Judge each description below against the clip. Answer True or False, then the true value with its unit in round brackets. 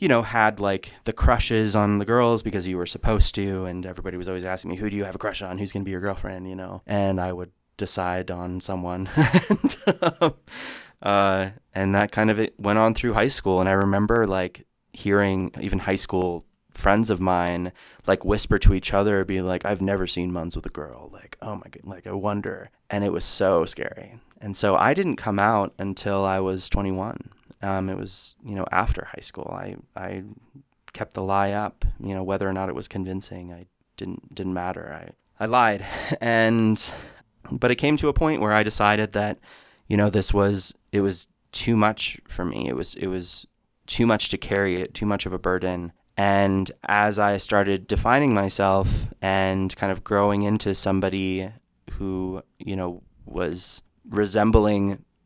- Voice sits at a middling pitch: False (100 Hz)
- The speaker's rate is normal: True (195 wpm)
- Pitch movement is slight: True (2.1 semitones)